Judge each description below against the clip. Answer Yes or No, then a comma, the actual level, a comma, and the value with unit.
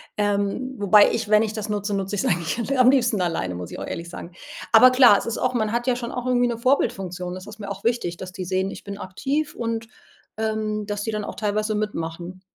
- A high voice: Yes, high, 210 Hz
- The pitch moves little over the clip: No, average, 3.7 semitones